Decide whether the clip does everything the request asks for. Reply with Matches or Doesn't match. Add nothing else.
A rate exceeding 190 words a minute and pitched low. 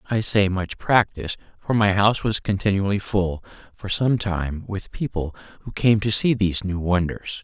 Doesn't match